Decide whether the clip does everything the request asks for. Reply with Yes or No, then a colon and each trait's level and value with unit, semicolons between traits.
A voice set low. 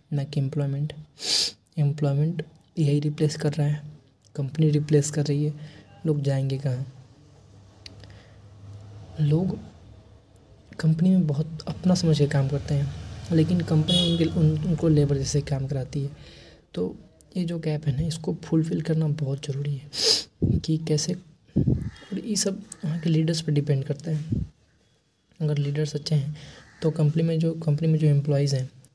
No: medium, 150 Hz